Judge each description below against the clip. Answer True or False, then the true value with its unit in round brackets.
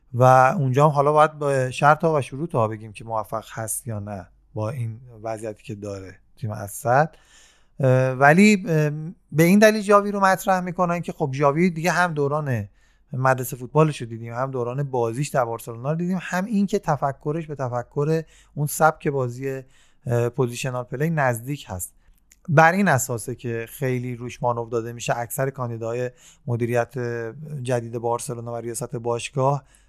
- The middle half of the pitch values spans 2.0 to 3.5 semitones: False (4.4 semitones)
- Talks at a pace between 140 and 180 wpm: True (155 wpm)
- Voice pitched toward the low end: True (130 Hz)